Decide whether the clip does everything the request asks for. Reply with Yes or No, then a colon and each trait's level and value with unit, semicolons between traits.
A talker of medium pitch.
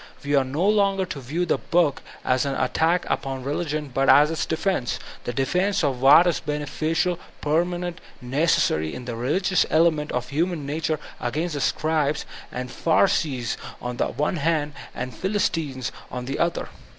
Yes: medium, 150 Hz